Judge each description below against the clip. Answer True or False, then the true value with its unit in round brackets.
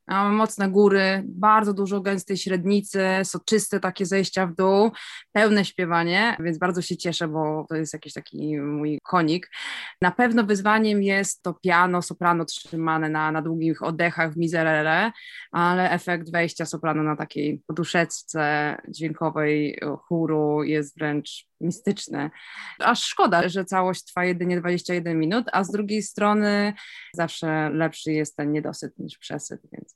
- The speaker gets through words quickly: False (140 wpm)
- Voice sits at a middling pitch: True (175 Hz)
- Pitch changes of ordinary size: True (3.8 semitones)